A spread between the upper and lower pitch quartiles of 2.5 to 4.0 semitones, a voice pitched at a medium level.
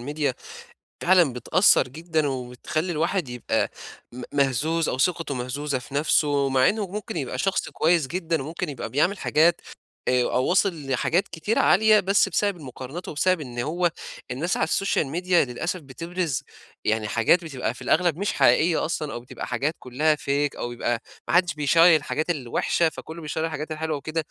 No: average, 4.5 semitones; medium, 155 Hz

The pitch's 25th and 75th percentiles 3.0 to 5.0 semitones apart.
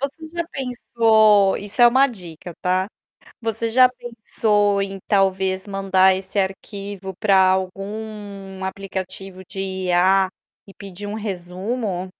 No: narrow, 2.4 semitones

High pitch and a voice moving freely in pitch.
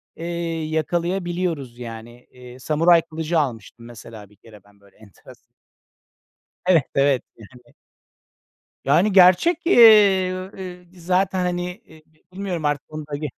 No: medium, 160 Hz; wide, 6.5 semitones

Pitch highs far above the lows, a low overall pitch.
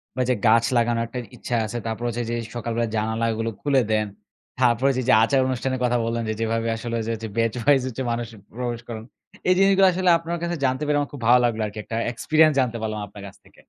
No: narrow, 2.5 semitones; low, 120 Hz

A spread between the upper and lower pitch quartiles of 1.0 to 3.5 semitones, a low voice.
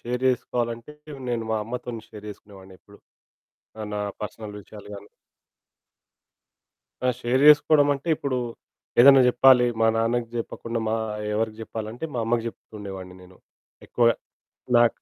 Yes: average, 2.7 semitones; low, 115 Hz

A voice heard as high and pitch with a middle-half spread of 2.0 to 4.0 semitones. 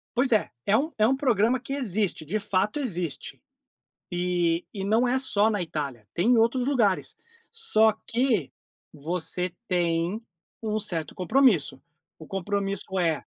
No: high, 200 Hz; average, 5.1 semitones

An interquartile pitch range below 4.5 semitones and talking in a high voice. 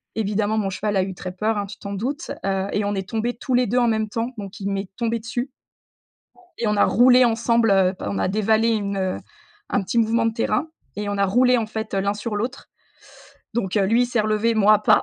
Yes: average, 2.7 semitones; high, 215 Hz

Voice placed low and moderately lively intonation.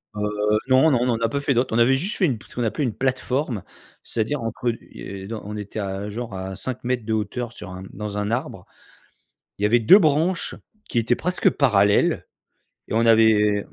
Yes: low, 115 Hz; average, 3.7 semitones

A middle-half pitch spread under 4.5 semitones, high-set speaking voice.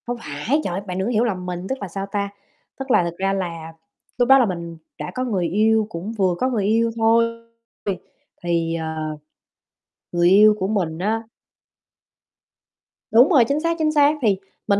No: average, 4.8 semitones; high, 200 Hz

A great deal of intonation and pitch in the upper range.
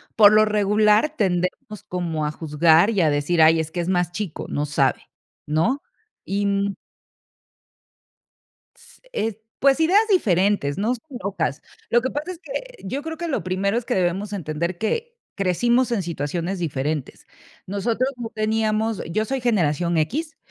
Yes: wide, 5.9 semitones; high, 200 Hz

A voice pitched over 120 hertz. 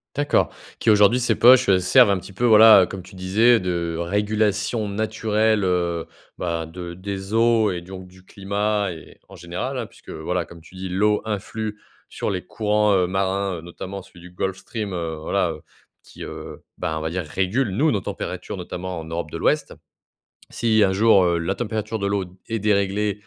No: low, 100 Hz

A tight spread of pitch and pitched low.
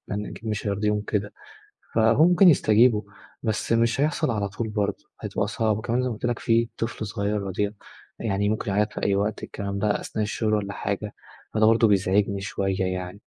Yes: narrow, 2.0 semitones; low, 105 Hz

